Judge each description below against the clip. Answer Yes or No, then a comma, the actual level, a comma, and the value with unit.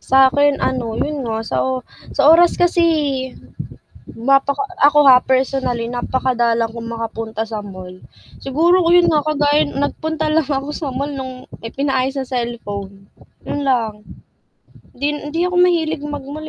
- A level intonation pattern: No, average, 4.1 semitones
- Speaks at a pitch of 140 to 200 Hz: No, very high, 270 Hz